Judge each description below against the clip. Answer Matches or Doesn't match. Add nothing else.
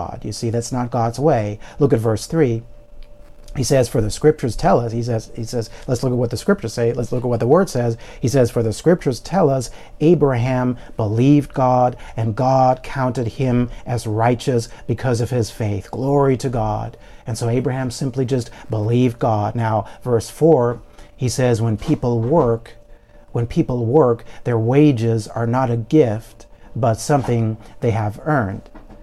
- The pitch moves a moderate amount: Doesn't match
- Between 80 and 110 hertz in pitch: Doesn't match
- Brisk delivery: Doesn't match